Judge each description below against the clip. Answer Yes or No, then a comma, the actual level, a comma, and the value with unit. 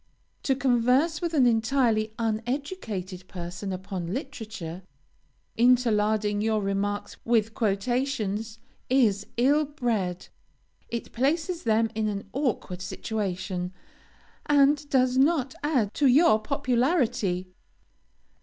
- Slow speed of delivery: Yes, slow, 100 wpm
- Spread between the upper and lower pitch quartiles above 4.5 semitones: Yes, average, 4.9 semitones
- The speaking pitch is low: No, high, 225 Hz